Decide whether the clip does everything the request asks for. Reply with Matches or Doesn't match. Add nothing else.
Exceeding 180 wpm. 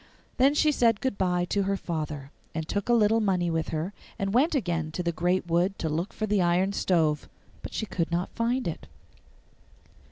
Matches